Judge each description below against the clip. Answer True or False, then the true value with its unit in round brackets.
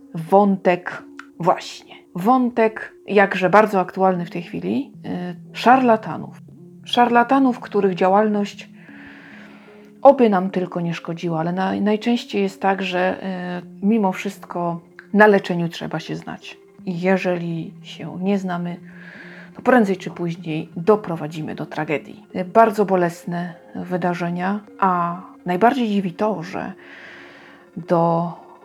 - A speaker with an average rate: False (105 wpm)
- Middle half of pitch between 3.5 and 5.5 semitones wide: False (2.9 semitones)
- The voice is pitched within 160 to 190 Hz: True (185 Hz)